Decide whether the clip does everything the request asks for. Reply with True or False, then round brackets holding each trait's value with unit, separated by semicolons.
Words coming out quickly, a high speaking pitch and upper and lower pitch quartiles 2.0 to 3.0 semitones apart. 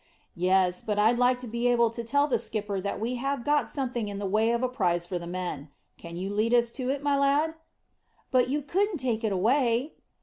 False (230 wpm; 235 Hz; 4.7 semitones)